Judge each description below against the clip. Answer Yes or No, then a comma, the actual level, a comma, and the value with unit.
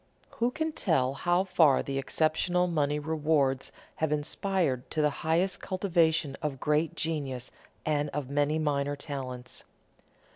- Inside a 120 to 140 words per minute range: Yes, slow, 135 wpm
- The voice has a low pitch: No, medium, 150 Hz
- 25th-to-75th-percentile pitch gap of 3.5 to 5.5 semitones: No, average, 3.1 semitones